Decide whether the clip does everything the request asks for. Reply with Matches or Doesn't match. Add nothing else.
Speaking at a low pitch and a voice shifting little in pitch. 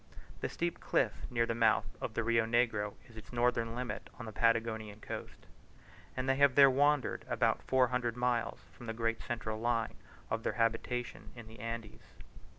Matches